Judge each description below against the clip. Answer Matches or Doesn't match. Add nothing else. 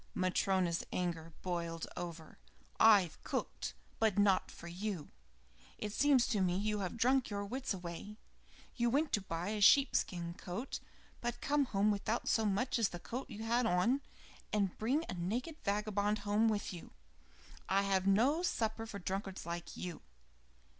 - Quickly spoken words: Doesn't match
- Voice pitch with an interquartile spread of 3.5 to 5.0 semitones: Matches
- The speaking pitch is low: Doesn't match